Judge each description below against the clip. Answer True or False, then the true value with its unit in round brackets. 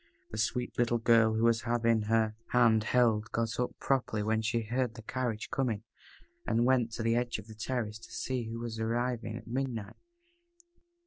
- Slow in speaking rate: False (185 wpm)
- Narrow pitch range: True (1.6 semitones)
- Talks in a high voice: False (115 Hz)